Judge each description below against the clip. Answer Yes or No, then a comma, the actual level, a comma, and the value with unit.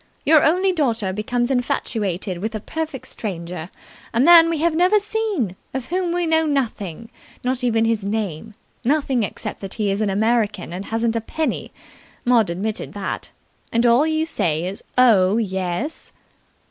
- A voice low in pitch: No, high, 230 Hz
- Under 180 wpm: Yes, average, 160 wpm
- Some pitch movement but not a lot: No, wide, 7.2 semitones